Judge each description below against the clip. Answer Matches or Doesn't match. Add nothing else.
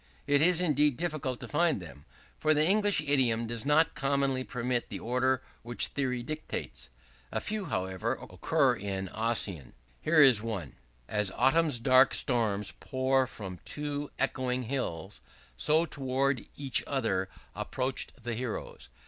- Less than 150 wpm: Matches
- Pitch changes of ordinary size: Matches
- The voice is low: Matches